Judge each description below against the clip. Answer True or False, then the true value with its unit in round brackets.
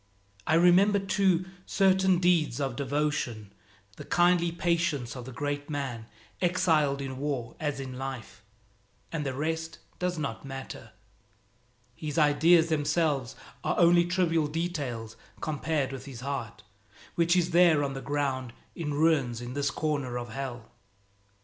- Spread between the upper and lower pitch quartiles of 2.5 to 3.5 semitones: False (4.2 semitones)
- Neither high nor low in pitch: True (145 Hz)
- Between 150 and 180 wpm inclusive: False (140 wpm)